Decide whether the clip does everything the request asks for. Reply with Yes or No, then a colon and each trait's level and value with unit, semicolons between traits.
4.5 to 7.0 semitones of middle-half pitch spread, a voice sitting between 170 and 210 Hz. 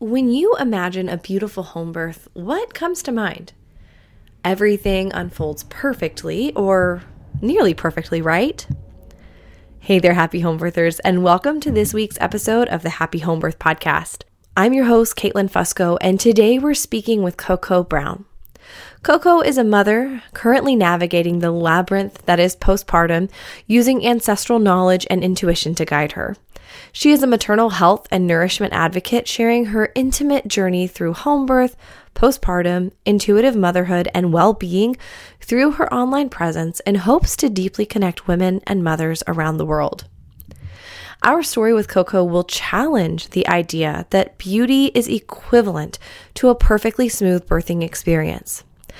Yes: average, 5.3 semitones; high, 190 Hz